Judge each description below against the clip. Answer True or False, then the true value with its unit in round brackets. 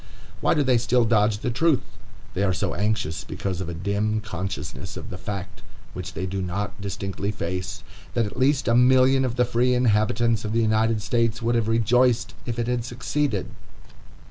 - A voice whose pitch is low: True (110 Hz)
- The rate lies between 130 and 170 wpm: False (190 wpm)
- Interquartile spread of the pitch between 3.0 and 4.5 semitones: True (3.7 semitones)